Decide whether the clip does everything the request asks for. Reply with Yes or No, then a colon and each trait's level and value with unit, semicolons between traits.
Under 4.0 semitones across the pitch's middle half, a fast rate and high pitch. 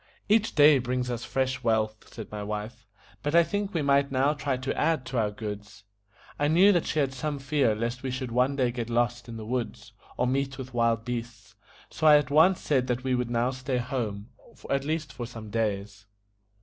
No: average, 3.4 semitones; fast, 215 wpm; low, 125 Hz